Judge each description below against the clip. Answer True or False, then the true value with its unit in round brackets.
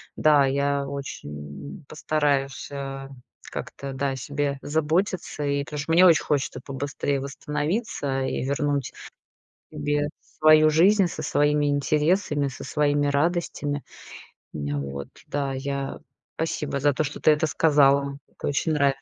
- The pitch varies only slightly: True (1.6 semitones)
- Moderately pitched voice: True (145 Hz)